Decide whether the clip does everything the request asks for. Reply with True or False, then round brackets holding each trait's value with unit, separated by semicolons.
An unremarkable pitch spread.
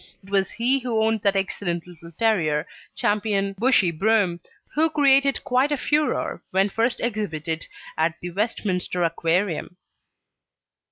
True (5.0 semitones)